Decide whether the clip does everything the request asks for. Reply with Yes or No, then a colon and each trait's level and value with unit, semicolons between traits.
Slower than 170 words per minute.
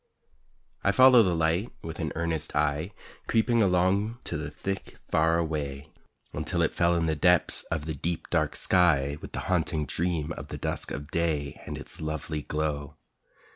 No: average, 175 wpm